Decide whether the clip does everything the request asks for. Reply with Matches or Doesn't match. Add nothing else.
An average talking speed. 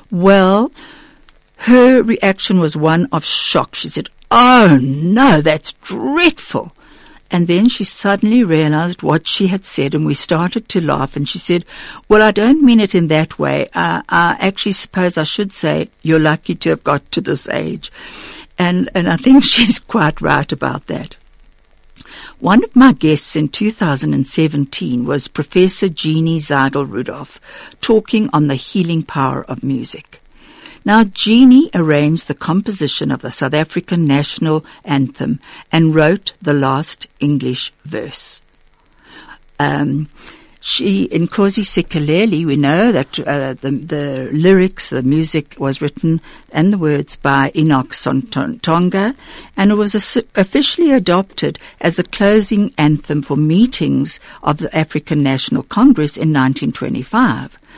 Matches